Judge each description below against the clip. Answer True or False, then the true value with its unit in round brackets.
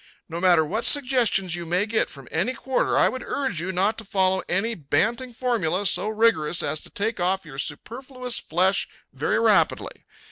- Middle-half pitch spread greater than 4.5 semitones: True (5.1 semitones)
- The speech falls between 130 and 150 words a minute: False (180 wpm)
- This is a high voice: True (195 Hz)